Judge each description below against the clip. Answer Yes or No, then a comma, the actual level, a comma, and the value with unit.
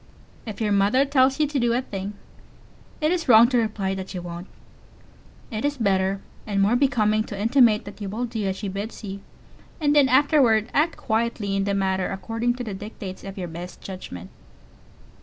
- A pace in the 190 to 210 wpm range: Yes, average, 195 wpm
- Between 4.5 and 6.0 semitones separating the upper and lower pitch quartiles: No, average, 4.0 semitones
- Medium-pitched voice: No, high, 215 Hz